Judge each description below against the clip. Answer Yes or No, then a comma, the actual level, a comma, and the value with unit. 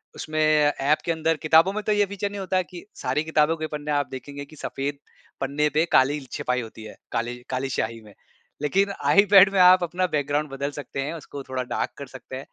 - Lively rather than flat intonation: No, average, 4.3 semitones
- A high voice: No, medium, 150 Hz